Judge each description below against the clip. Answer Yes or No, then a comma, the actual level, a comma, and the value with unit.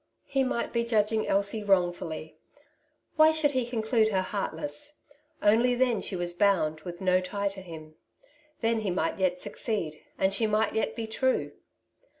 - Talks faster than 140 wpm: Yes, average, 160 wpm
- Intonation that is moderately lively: Yes, average, 4.3 semitones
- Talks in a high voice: Yes, high, 210 Hz